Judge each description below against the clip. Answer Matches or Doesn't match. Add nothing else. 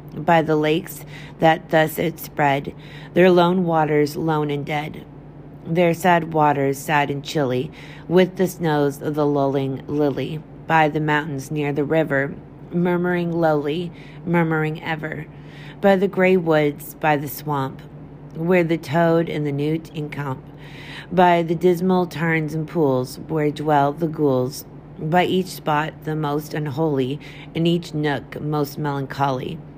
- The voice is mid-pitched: Matches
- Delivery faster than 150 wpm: Doesn't match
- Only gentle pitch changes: Matches